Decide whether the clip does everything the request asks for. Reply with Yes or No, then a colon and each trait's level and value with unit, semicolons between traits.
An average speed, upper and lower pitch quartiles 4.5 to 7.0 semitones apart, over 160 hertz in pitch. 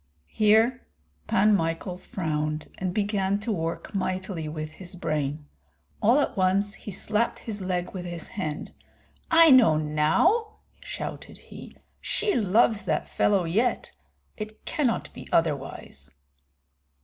No: slow, 125 wpm; average, 4.9 semitones; high, 190 Hz